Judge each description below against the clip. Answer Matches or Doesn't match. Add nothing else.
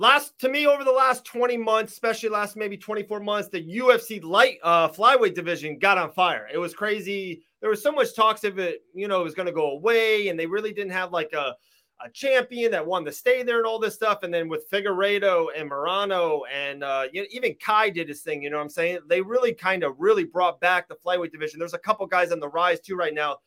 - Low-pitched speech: Doesn't match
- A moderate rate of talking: Doesn't match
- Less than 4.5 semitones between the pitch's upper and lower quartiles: Doesn't match